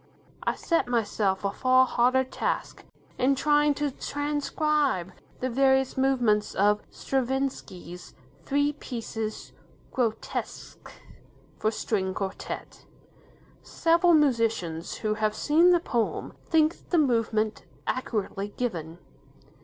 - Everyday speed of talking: No, slow, 105 wpm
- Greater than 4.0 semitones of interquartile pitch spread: Yes, average, 5.2 semitones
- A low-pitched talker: No, very high, 250 Hz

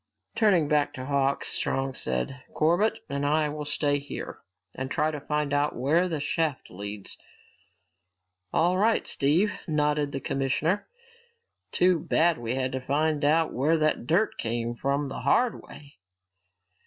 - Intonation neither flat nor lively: Yes, average, 3.0 semitones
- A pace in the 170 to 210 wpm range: No, average, 150 wpm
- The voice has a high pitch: No, medium, 145 Hz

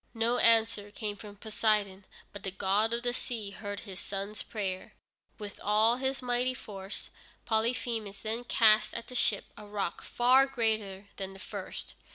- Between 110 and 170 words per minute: Yes, average, 165 wpm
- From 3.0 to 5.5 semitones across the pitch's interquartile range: No, narrow, 2.6 semitones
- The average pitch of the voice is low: No, high, 215 Hz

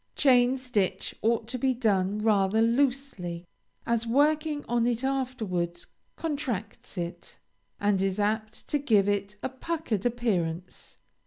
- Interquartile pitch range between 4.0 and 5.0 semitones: Yes, average, 4.7 semitones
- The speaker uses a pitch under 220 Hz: No, high, 225 Hz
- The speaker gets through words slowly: Yes, slow, 130 wpm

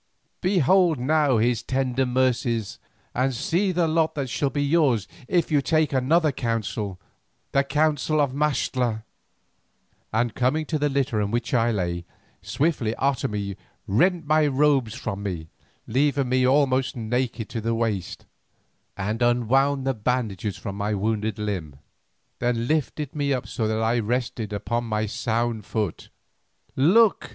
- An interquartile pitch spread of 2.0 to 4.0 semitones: No, average, 4.6 semitones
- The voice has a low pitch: Yes, low, 125 Hz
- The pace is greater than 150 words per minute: No, average, 145 wpm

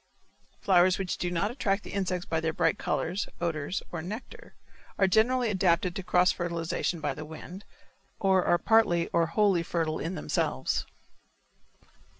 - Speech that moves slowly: No, average, 155 wpm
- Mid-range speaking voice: Yes, medium, 180 Hz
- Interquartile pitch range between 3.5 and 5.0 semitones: No, average, 2.7 semitones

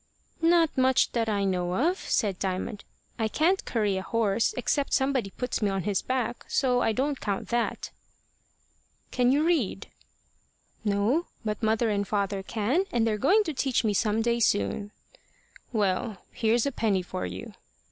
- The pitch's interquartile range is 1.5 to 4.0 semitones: No, average, 4.5 semitones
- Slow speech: No, average, 165 wpm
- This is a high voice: Yes, high, 225 Hz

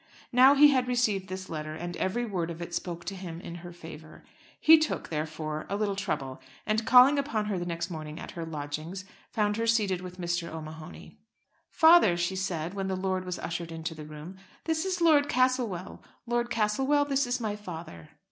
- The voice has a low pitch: No, medium, 185 Hz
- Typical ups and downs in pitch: No, wide, 6.3 semitones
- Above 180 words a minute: Yes, average, 195 wpm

